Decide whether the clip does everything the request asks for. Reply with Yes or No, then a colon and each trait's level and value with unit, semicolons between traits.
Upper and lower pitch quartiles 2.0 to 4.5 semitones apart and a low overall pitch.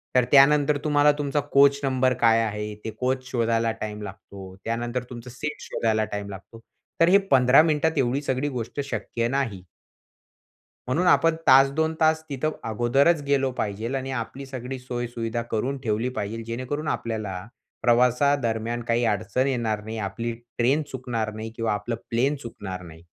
Yes: average, 3.5 semitones; low, 120 Hz